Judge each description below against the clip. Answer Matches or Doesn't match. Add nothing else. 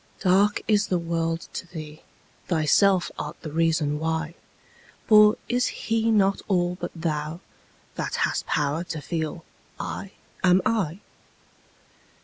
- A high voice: Doesn't match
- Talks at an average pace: Doesn't match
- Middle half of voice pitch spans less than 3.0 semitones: Doesn't match